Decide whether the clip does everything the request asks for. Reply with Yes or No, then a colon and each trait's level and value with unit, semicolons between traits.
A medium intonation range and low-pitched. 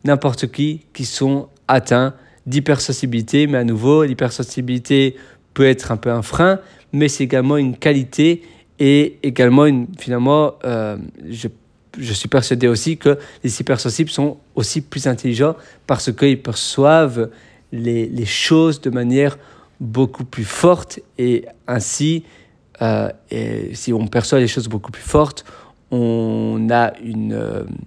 Yes: average, 3.2 semitones; low, 130 Hz